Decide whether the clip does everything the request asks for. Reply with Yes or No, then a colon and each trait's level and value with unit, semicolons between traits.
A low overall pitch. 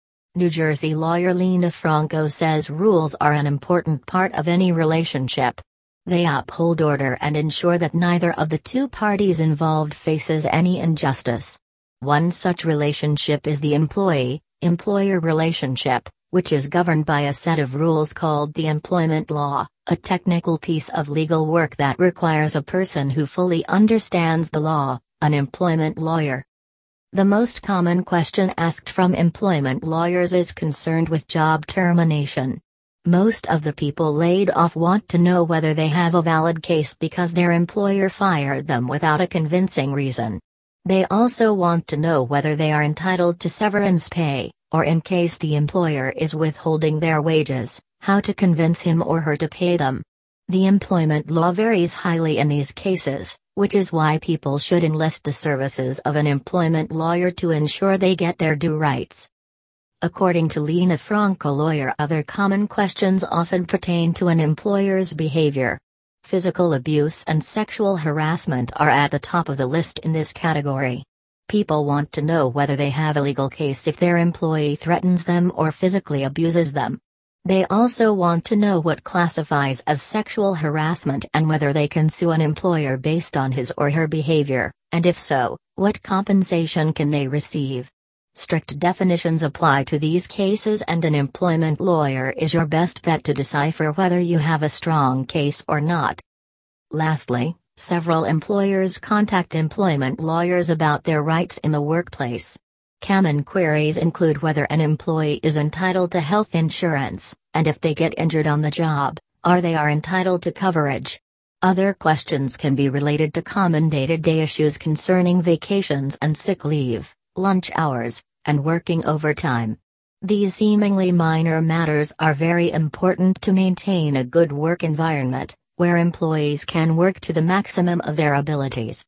No: medium, 160 Hz